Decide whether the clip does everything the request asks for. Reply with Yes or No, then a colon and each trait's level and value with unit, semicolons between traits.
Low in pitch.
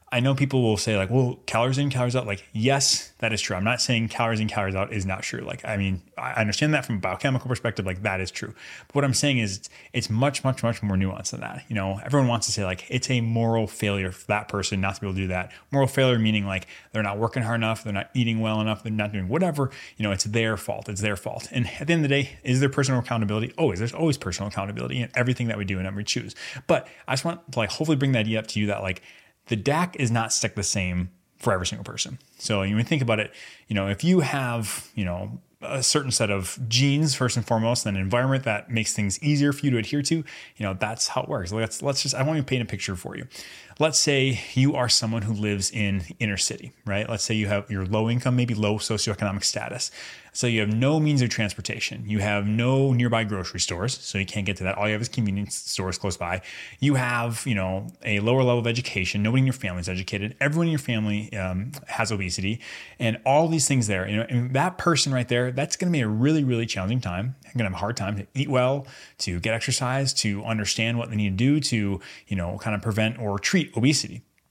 Yes: low, 115 Hz